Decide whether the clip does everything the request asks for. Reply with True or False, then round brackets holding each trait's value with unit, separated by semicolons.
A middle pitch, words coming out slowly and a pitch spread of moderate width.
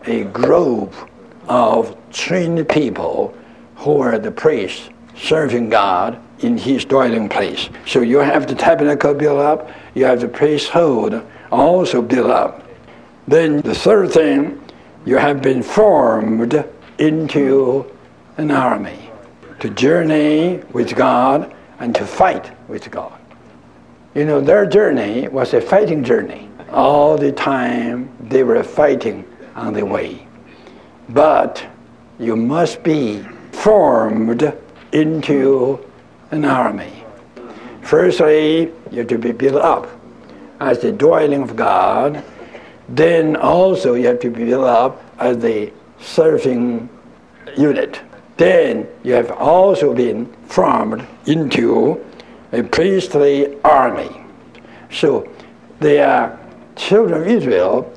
True (145 Hz; 120 wpm; 4.7 semitones)